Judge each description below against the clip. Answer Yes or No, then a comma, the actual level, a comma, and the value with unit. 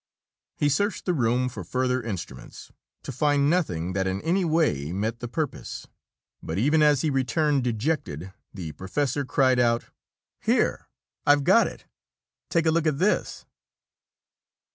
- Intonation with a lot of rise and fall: Yes, wide, 6.6 semitones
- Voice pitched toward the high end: No, low, 130 Hz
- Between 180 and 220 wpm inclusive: No, average, 145 wpm